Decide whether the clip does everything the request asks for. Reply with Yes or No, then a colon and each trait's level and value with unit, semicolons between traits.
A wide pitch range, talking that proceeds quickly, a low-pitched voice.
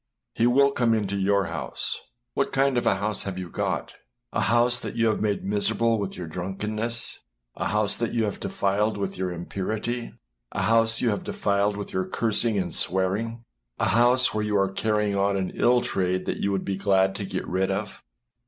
No: average, 3.0 semitones; fast, 210 wpm; low, 105 Hz